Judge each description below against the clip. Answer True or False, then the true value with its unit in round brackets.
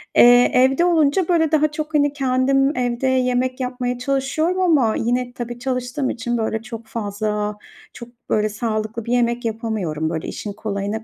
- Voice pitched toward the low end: False (245 Hz)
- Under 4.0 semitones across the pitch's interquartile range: True (3.5 semitones)